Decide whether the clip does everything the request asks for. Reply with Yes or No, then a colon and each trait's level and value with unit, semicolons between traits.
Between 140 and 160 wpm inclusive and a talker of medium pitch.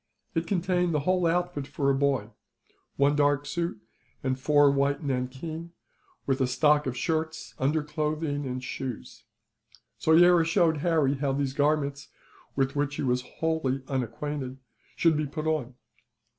Yes: average, 145 wpm; medium, 145 Hz